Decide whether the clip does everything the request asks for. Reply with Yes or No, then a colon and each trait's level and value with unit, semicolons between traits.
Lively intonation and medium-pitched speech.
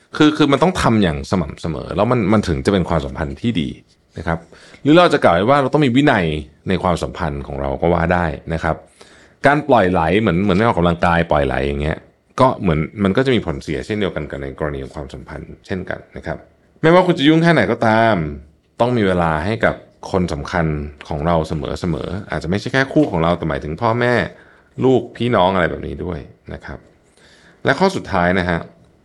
No: wide, 6.7 semitones; very low, 85 Hz